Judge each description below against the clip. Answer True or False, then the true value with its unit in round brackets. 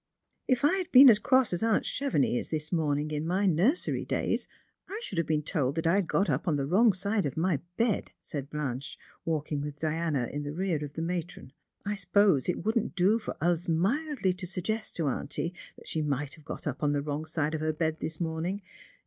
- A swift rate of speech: True (230 wpm)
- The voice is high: False (165 Hz)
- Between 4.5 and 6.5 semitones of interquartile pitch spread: True (5.1 semitones)